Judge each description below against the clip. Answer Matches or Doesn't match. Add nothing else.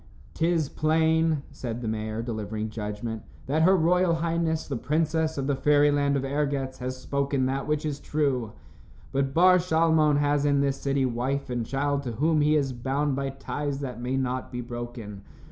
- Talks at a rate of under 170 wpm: Doesn't match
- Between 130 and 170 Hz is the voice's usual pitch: Matches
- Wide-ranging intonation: Doesn't match